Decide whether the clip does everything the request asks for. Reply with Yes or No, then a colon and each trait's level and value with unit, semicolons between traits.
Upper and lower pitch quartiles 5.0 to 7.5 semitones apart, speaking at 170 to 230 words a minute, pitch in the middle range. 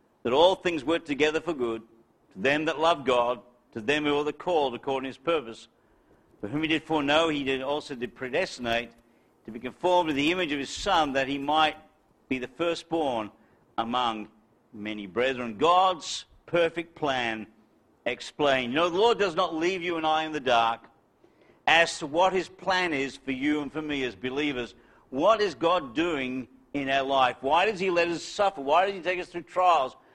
Yes: average, 5.3 semitones; average, 200 wpm; medium, 145 Hz